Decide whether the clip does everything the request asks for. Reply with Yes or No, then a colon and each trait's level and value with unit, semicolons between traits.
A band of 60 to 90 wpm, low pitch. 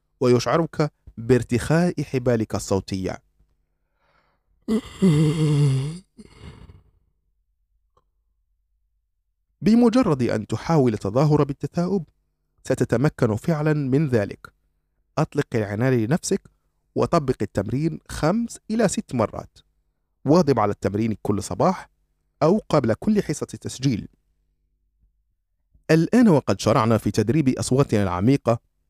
Yes: average, 80 wpm; low, 115 Hz